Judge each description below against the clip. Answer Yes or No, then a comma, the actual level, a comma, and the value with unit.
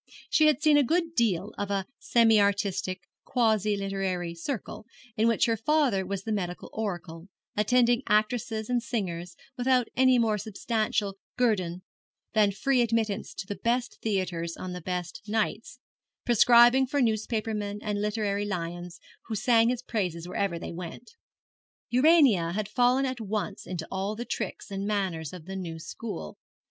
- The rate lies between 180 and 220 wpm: No, average, 155 wpm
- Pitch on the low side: No, high, 210 Hz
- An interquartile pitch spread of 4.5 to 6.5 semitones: No, average, 4.0 semitones